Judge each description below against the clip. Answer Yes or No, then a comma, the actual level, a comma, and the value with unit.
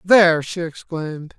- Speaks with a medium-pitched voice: Yes, medium, 170 Hz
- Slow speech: Yes, slow, 130 wpm